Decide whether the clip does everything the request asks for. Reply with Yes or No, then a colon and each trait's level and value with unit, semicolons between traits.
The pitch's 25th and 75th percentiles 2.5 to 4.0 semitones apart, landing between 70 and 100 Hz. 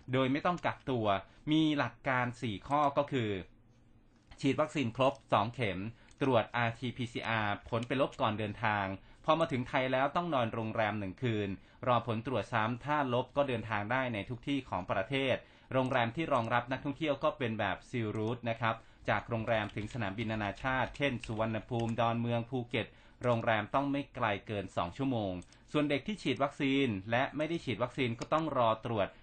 No: average, 3.5 semitones; low, 120 Hz